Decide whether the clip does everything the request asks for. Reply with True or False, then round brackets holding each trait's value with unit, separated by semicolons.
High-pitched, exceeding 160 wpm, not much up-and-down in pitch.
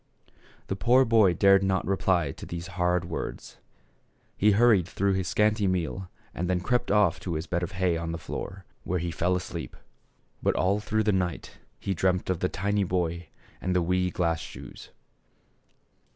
False (90 Hz; 180 wpm; 2.1 semitones)